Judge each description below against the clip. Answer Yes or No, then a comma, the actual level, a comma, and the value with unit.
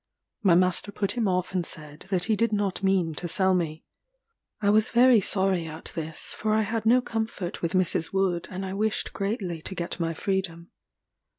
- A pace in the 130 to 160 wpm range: No, average, 195 wpm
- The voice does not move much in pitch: No, average, 3.4 semitones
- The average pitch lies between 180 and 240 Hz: Yes, high, 190 Hz